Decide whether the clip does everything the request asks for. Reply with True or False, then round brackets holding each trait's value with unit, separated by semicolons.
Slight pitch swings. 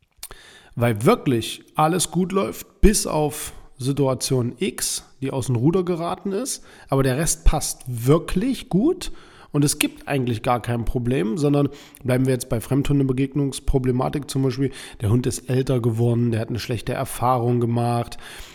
False (3.9 semitones)